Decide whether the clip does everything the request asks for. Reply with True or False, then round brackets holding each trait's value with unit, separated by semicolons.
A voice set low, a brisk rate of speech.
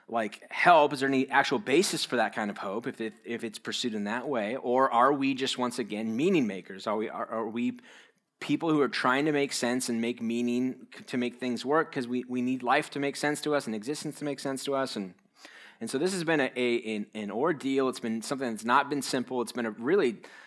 True (125 Hz; 250 wpm)